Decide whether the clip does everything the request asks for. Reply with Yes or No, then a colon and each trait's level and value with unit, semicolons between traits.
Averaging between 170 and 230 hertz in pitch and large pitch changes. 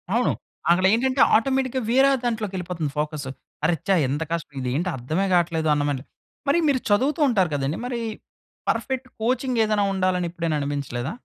Yes: medium, 185 Hz; wide, 8.1 semitones